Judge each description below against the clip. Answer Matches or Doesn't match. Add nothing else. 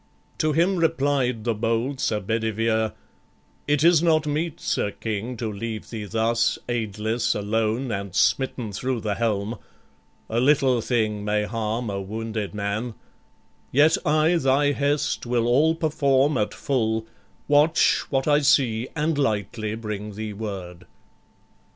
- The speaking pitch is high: Doesn't match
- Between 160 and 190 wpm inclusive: Doesn't match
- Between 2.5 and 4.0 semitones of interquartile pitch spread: Doesn't match